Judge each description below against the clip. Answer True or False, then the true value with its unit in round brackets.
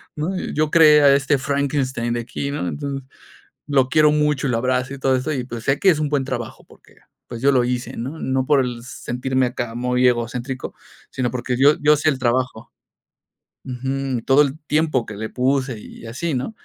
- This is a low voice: True (130 Hz)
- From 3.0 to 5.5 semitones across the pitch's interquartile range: False (2.5 semitones)